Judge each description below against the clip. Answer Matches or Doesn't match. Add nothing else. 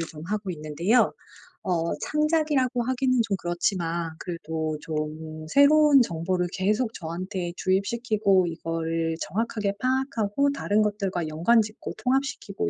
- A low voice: Doesn't match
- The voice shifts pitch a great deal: Matches